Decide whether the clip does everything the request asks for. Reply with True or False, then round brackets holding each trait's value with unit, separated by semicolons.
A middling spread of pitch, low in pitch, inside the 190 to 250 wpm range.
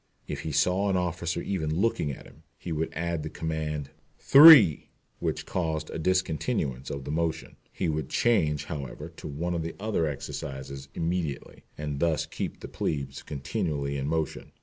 False (3.2 semitones; 80 Hz; 170 wpm)